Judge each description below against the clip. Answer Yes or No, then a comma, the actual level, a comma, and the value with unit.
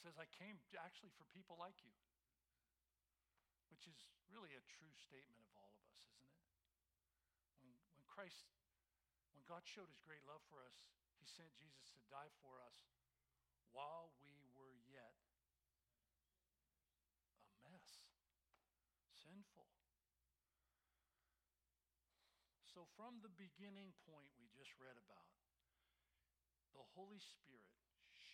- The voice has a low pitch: Yes, very low, 80 Hz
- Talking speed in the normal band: No, slow, 120 wpm